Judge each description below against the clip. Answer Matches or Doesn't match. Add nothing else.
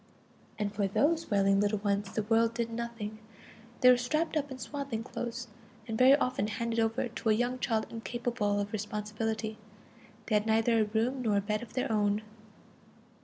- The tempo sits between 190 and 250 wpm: Doesn't match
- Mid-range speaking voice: Doesn't match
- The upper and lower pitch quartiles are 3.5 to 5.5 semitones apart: Doesn't match